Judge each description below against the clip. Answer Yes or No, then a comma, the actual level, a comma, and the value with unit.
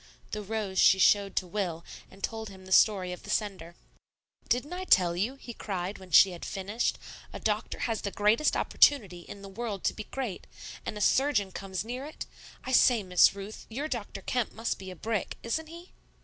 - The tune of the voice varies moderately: Yes, average, 3.7 semitones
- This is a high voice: Yes, high, 205 Hz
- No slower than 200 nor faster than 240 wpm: Yes, fast, 205 wpm